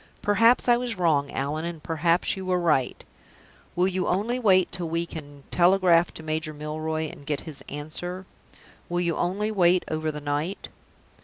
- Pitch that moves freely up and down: No, average, 3.1 semitones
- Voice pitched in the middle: Yes, medium, 170 Hz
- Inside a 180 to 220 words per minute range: No, average, 170 wpm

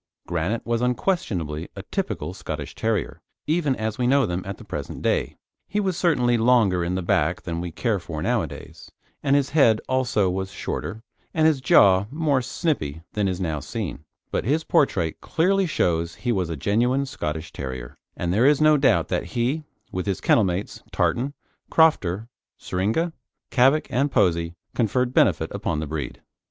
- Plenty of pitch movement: Yes, wide, 7.9 semitones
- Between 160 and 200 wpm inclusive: Yes, average, 170 wpm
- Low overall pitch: Yes, low, 110 Hz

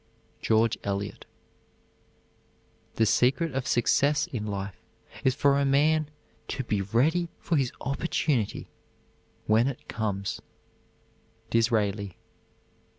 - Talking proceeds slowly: Yes, slow, 100 wpm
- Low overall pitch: Yes, low, 120 Hz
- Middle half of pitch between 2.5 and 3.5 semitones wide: No, average, 5.1 semitones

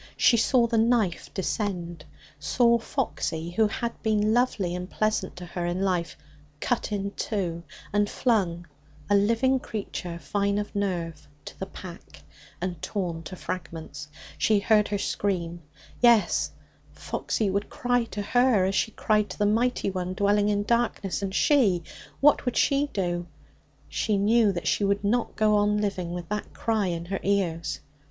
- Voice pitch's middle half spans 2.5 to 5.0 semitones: Yes, average, 3.7 semitones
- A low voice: No, high, 200 Hz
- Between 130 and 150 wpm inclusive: No, average, 165 wpm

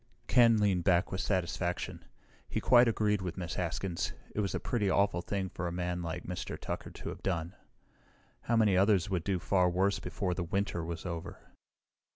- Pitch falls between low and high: No, very low, 95 Hz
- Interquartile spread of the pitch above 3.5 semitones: No, narrow, 2.4 semitones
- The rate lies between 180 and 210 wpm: Yes, average, 190 wpm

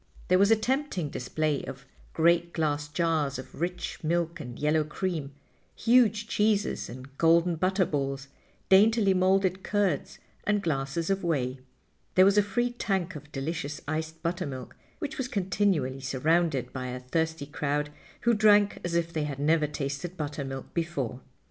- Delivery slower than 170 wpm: Yes, average, 155 wpm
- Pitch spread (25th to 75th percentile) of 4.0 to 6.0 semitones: Yes, average, 5.0 semitones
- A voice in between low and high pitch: Yes, medium, 165 Hz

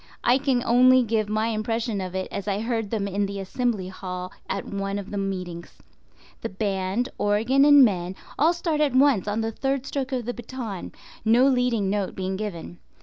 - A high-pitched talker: Yes, high, 215 Hz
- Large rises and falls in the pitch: No, average, 4.3 semitones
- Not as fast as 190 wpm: No, average, 195 wpm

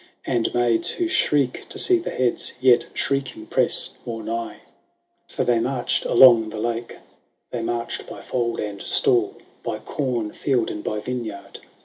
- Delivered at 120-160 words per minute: Yes, average, 155 wpm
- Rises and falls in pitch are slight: Yes, narrow, 2.2 semitones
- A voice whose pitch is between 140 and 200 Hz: No, low, 120 Hz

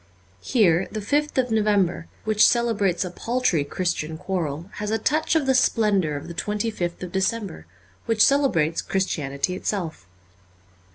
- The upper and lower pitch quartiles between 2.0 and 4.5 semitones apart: No, average, 4.9 semitones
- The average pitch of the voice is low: No, high, 195 Hz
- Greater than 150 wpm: No, average, 145 wpm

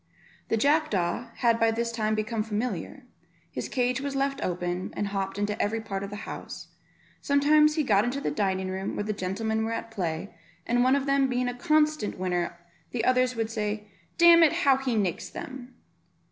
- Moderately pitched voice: No, high, 225 Hz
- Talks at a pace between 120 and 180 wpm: No, average, 195 wpm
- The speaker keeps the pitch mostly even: No, average, 4.6 semitones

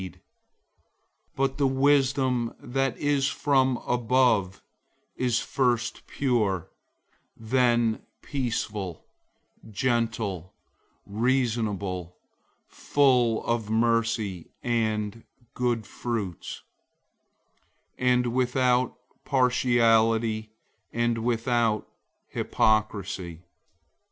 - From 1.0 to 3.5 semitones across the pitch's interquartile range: Yes, narrow, 2.6 semitones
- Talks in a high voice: No, low, 120 Hz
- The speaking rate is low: Yes, slow, 65 wpm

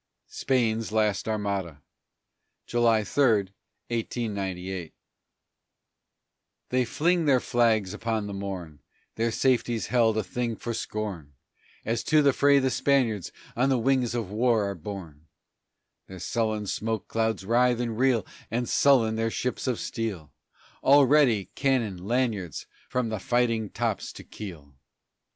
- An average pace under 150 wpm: Yes, slow, 135 wpm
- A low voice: Yes, low, 115 Hz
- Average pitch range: Yes, average, 3.5 semitones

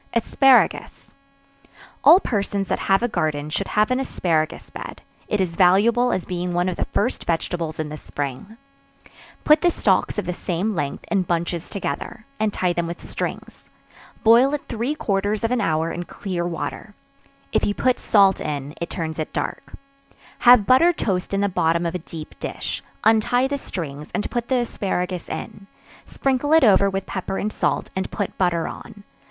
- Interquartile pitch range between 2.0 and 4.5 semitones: No, average, 5.0 semitones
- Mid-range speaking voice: No, high, 195 Hz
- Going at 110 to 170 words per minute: No, average, 180 wpm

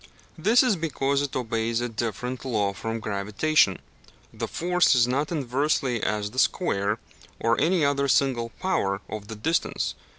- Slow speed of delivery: No, average, 155 wpm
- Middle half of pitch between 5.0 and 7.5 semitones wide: Yes, wide, 5.4 semitones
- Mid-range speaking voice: No, low, 125 Hz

